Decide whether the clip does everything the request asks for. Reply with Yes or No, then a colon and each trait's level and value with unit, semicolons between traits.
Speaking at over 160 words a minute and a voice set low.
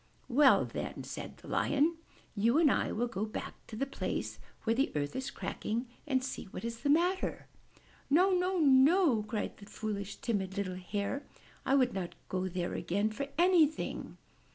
No: average, 175 wpm; high, 240 Hz